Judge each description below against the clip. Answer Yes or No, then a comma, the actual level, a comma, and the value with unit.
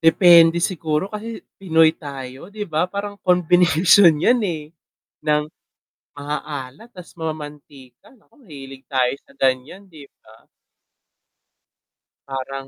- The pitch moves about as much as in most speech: Yes, average, 4.5 semitones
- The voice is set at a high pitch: No, medium, 160 Hz